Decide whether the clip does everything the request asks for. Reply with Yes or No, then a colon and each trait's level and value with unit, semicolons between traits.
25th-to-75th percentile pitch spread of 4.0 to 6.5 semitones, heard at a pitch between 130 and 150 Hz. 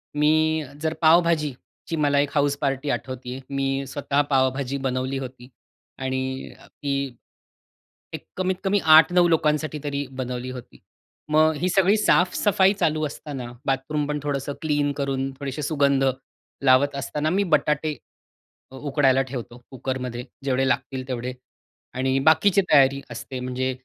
No: average, 2.9 semitones; medium, 140 Hz